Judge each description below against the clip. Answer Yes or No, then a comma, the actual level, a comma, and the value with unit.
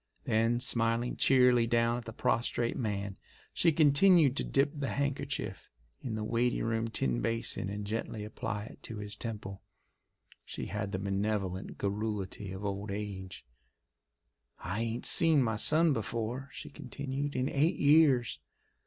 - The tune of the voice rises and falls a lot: No, average, 4.2 semitones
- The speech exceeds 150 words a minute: No, average, 145 wpm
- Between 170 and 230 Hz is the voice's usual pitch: No, low, 115 Hz